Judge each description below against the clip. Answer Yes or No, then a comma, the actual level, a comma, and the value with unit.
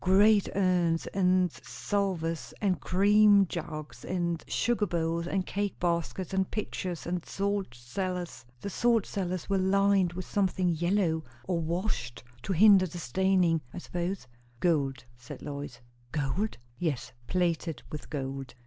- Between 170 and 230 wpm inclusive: No, slow, 135 wpm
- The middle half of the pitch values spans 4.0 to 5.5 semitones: No, average, 3.2 semitones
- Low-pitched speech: No, medium, 180 Hz